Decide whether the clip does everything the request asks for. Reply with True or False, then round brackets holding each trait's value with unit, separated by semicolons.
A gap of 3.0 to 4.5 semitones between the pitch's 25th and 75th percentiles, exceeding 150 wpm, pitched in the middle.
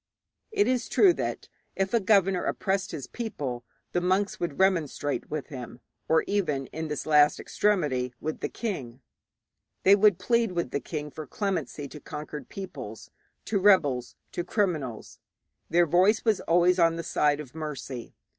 False (5.1 semitones; 160 wpm; 165 Hz)